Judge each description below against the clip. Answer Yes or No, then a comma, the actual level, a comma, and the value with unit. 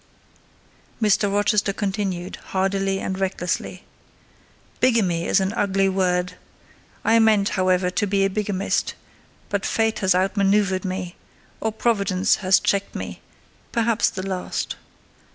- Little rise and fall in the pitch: Yes, narrow, 1.7 semitones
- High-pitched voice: Yes, high, 195 Hz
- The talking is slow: Yes, slow, 115 wpm